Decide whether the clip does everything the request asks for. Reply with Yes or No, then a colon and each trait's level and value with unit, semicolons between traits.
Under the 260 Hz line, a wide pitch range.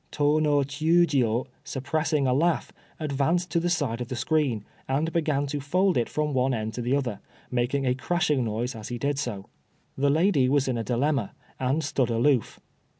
No: medium, 140 Hz; average, 3.7 semitones